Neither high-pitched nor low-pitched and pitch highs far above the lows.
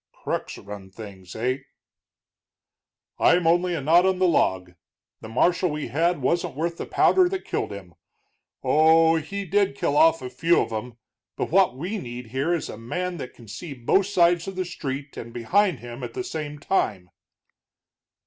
Yes: medium, 155 Hz; wide, 6.7 semitones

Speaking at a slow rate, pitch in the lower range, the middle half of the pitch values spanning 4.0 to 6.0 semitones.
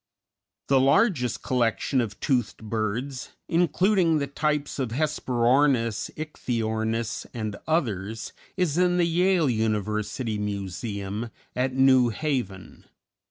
Yes: slow, 105 wpm; low, 125 Hz; average, 5.3 semitones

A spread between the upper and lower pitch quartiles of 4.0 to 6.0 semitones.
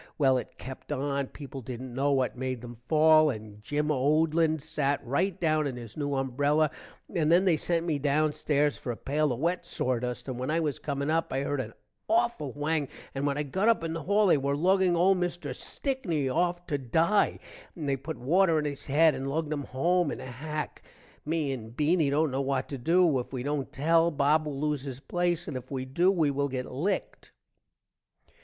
No: average, 3.3 semitones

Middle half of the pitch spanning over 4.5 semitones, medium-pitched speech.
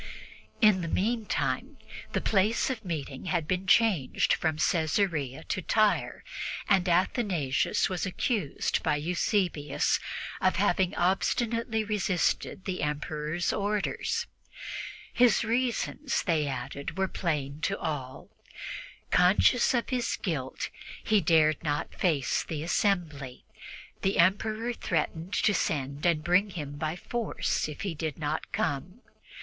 Yes: average, 5.2 semitones; medium, 175 Hz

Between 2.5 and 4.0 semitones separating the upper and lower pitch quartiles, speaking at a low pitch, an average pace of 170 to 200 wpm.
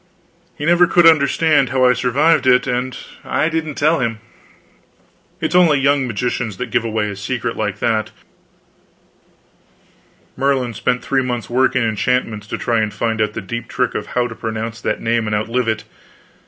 Yes: average, 3.4 semitones; low, 125 Hz; average, 175 wpm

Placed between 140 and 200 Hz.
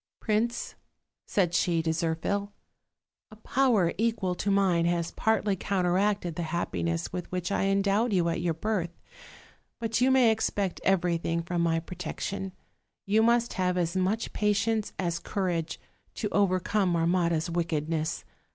Yes: medium, 185 Hz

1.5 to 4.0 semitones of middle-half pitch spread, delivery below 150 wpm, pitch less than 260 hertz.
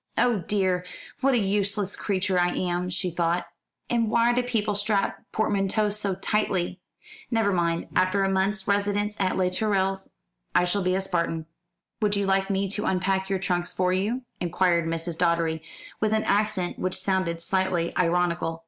No: narrow, 2.5 semitones; average, 165 wpm; high, 190 Hz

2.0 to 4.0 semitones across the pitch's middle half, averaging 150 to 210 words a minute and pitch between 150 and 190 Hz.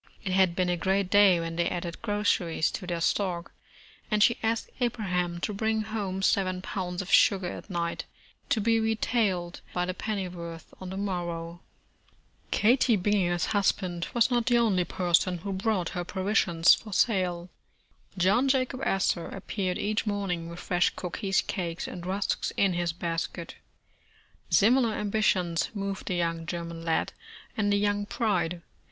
Yes: average, 3.2 semitones; average, 160 wpm; medium, 185 Hz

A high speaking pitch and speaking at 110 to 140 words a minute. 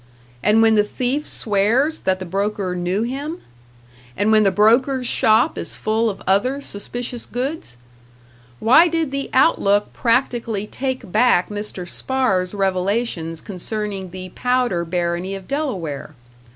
Yes: high, 215 Hz; slow, 135 wpm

